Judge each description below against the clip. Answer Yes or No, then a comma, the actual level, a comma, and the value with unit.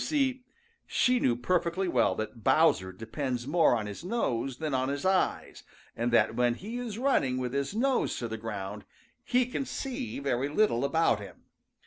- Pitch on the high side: No, medium, 140 Hz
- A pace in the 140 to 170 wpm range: No, average, 180 wpm